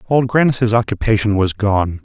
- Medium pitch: No, low, 110 Hz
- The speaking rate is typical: Yes, average, 145 wpm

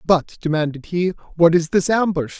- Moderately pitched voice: Yes, medium, 170 Hz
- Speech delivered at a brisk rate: No, average, 175 wpm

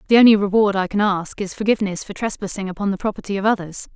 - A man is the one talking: No, female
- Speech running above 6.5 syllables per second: Yes, 7.1 syllables/s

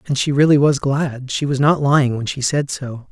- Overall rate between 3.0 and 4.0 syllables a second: No, 5.1 syllables/s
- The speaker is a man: Yes, male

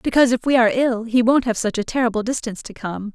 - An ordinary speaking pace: No, fast, 265 wpm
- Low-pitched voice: No, high, 235 Hz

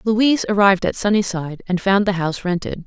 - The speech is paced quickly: No, average, 190 wpm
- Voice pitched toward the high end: Yes, high, 195 Hz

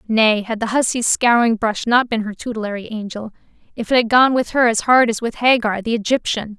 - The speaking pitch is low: No, high, 225 Hz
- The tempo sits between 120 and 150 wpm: No, average, 200 wpm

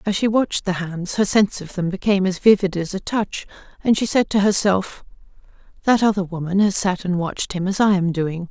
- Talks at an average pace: No, fast, 225 wpm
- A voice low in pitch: No, high, 190 Hz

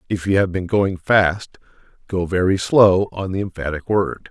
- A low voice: Yes, very low, 95 Hz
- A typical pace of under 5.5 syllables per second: Yes, 4.6 syllables/s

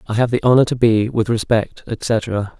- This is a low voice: Yes, low, 115 Hz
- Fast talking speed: Yes, fast, 210 wpm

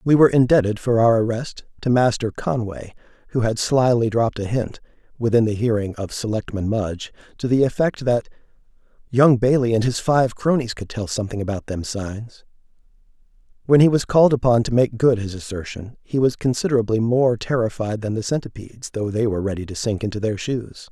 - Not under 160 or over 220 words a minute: Yes, average, 185 wpm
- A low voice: Yes, low, 115 Hz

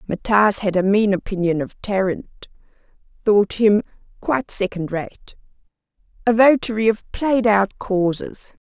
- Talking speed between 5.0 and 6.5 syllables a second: No, 4.2 syllables/s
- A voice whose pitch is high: Yes, high, 205 Hz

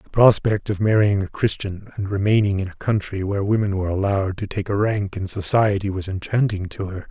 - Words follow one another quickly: Yes, fast, 210 wpm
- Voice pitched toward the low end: Yes, low, 100 Hz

